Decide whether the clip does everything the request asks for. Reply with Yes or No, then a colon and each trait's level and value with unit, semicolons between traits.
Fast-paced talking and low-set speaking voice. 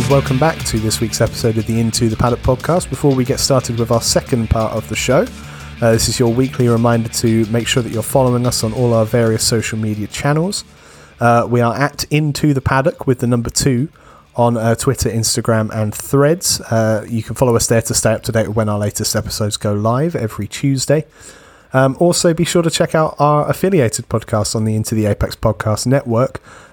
Yes: fast, 220 wpm; low, 120 Hz